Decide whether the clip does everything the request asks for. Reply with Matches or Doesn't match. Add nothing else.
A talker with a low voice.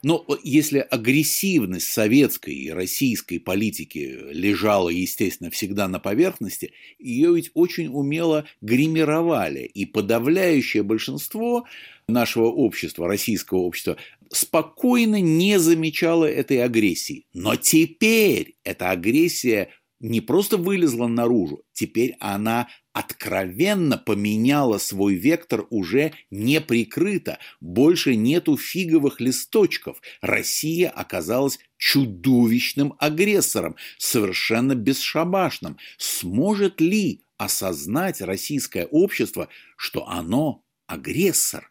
Doesn't match